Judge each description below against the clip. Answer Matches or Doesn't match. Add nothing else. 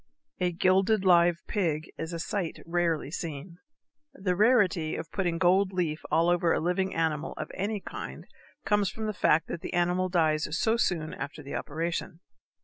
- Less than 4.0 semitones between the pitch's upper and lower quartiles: Matches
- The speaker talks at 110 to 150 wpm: Doesn't match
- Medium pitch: Matches